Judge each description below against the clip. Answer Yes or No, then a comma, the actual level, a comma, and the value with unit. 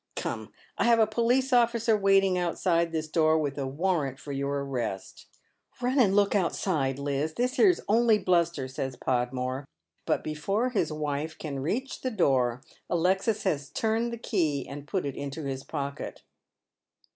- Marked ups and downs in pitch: Yes, wide, 7.3 semitones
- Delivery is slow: No, average, 155 wpm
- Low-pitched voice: No, medium, 165 Hz